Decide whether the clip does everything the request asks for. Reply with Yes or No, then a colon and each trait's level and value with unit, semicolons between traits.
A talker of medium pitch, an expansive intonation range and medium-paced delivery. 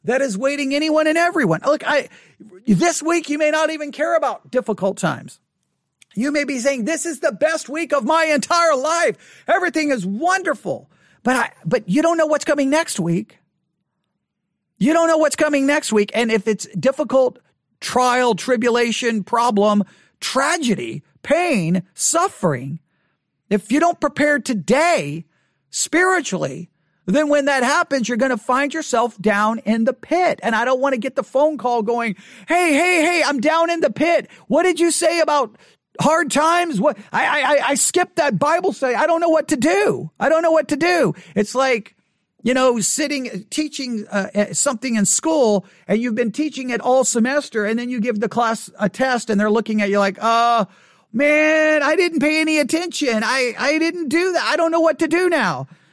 No: very high, 265 Hz; wide, 6.4 semitones; average, 190 wpm